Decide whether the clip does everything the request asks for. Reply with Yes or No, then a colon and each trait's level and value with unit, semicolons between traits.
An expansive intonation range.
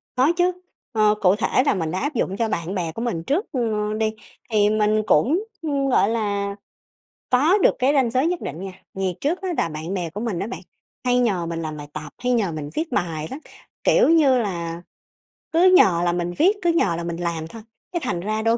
Yes: wide, 7.1 semitones